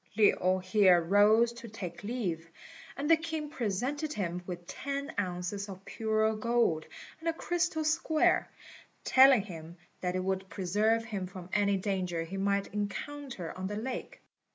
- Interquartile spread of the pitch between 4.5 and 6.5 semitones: Yes, average, 5.1 semitones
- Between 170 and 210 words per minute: No, average, 155 wpm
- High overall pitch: Yes, high, 205 Hz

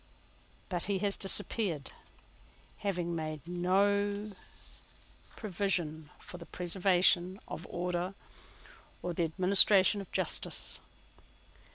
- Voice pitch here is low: No, medium, 180 Hz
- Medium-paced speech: No, slow, 90 wpm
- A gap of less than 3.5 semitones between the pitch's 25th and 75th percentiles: Yes, narrow, 2.5 semitones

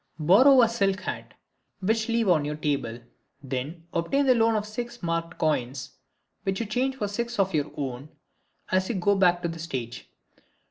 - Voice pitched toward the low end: No, medium, 185 Hz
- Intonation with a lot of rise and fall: Yes, wide, 6.8 semitones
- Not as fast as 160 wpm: No, average, 180 wpm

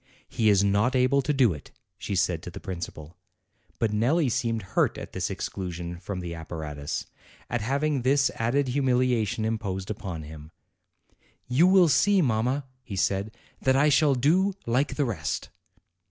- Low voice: Yes, low, 115 Hz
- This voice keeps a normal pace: Yes, average, 170 wpm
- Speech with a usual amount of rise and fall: No, wide, 6.6 semitones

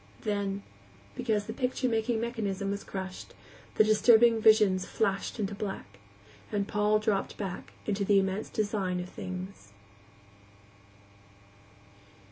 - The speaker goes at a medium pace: No, slow, 115 wpm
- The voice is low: No, high, 205 Hz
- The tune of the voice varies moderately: No, narrow, 2.1 semitones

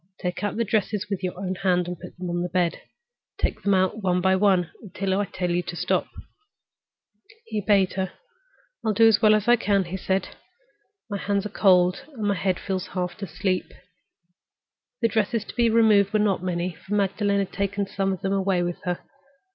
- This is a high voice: Yes, high, 195 Hz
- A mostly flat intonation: Yes, narrow, 2.1 semitones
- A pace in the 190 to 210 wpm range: Yes, fast, 205 wpm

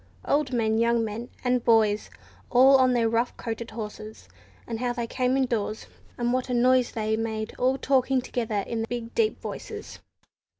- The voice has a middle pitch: No, high, 235 Hz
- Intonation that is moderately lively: No, narrow, 2.2 semitones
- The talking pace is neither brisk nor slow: Yes, average, 175 wpm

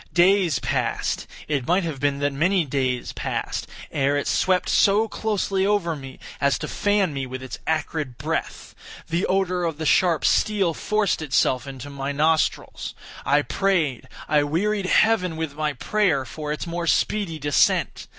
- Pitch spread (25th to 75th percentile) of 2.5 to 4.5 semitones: No, average, 5.0 semitones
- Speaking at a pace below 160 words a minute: Yes, average, 150 wpm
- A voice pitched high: No, medium, 160 Hz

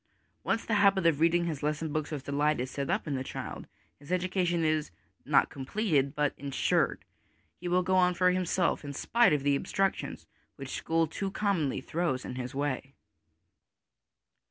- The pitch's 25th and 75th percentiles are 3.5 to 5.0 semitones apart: Yes, average, 4.4 semitones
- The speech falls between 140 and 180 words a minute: Yes, average, 175 wpm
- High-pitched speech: No, medium, 160 Hz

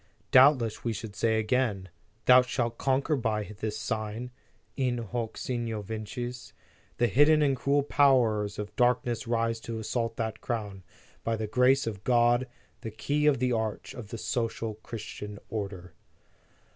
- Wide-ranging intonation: No, narrow, 2.6 semitones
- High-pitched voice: No, low, 115 Hz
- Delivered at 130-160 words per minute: Yes, average, 150 wpm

